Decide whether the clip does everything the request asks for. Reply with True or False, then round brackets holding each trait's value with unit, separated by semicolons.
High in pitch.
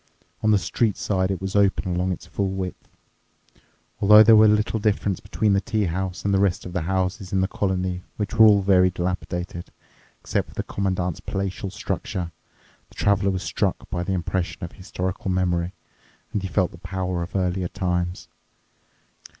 False (95 Hz)